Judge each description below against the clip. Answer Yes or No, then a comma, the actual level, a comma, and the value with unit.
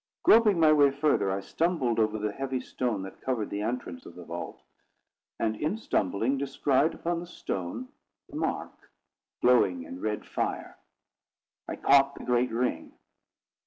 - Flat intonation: No, wide, 5.4 semitones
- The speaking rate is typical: Yes, average, 155 wpm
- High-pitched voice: No, low, 125 Hz